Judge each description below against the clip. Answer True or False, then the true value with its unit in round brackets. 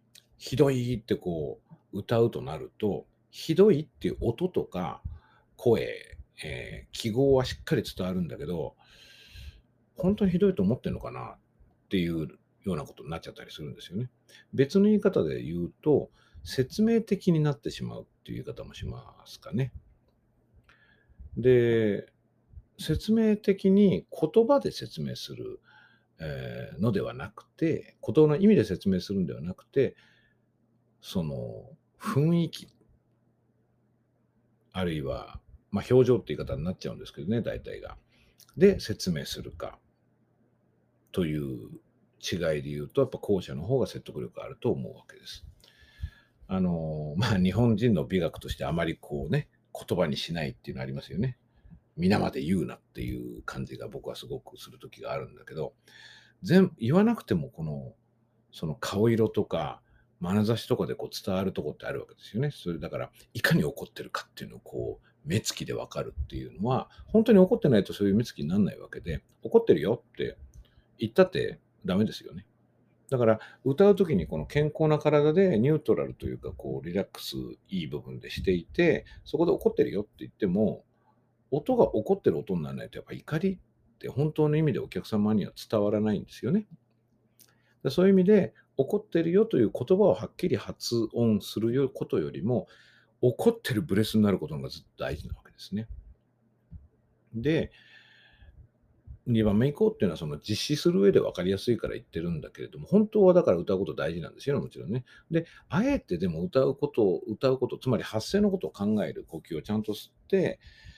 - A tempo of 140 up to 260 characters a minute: False (345 characters per minute)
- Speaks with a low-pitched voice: True (120 Hz)